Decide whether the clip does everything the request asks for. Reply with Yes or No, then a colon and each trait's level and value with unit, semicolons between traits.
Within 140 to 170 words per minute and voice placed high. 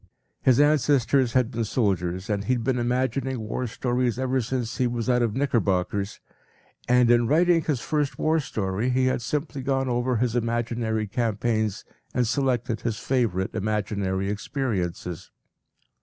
No: average, 150 wpm; low, 120 Hz